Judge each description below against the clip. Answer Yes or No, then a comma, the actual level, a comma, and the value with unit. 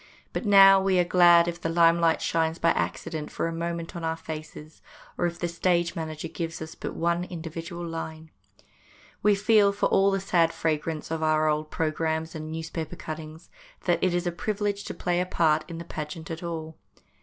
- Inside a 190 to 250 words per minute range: Yes, average, 195 wpm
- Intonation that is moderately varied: No, narrow, 1.7 semitones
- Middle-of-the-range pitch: Yes, medium, 165 Hz